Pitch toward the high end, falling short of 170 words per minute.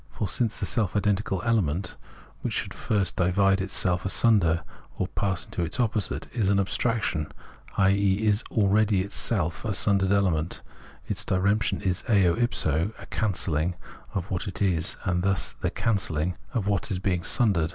No: very low, 95 Hz; average, 160 wpm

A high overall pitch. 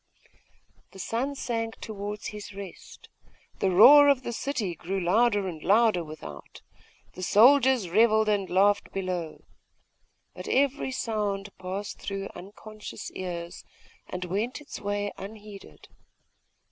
Yes: high, 205 Hz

